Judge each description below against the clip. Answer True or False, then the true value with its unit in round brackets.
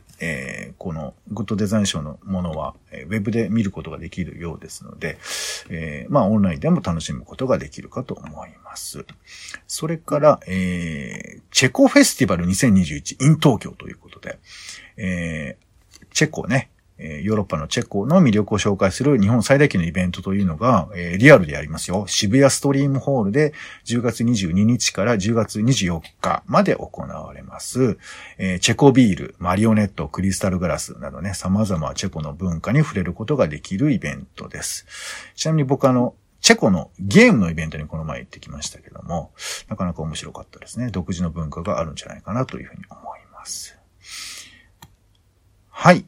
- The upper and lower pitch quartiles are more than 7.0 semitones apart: False (5.6 semitones)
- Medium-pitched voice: False (100 Hz)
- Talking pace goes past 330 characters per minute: True (365 characters per minute)